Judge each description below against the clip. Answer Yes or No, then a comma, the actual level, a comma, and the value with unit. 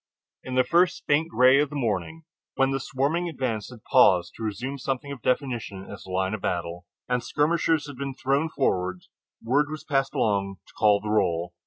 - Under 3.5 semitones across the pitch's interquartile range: No, wide, 5.6 semitones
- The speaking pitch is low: Yes, low, 130 Hz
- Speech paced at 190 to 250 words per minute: Yes, average, 195 wpm